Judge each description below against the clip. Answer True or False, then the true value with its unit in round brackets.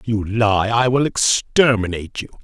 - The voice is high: False (110 Hz)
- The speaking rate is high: False (170 wpm)